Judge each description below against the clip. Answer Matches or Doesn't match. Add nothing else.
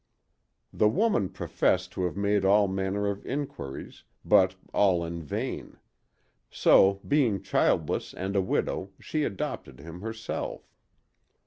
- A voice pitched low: Matches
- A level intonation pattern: Matches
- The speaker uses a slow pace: Matches